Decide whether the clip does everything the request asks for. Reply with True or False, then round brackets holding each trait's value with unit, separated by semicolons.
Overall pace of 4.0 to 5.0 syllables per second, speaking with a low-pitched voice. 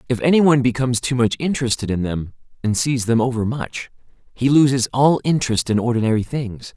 False (6.1 syllables/s; 125 Hz)